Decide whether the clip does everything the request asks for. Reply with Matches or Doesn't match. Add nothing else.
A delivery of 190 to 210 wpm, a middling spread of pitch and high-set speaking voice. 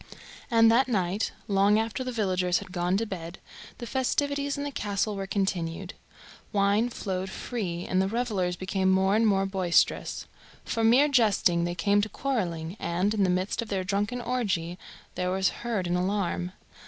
Doesn't match